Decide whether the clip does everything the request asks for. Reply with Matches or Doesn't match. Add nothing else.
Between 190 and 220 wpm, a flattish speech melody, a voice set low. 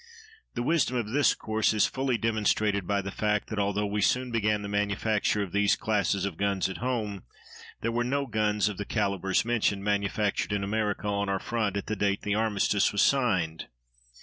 Matches